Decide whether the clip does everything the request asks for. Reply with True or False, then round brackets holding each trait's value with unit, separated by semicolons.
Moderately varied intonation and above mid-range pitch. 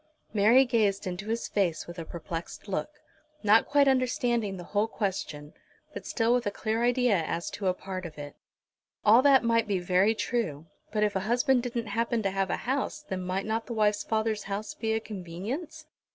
True (3.9 semitones; 215 Hz)